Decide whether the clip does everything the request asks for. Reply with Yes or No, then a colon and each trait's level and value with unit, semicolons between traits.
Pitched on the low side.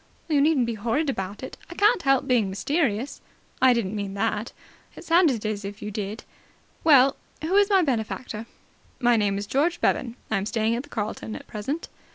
No: high, 235 Hz